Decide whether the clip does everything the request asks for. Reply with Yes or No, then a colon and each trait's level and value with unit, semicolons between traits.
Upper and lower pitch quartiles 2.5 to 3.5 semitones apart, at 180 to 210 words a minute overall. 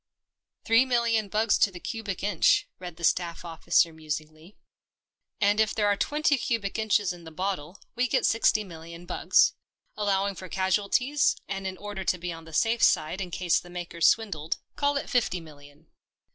No: average, 4.4 semitones; average, 185 wpm